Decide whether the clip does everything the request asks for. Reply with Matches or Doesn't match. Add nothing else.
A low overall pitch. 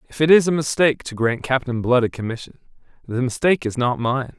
Matches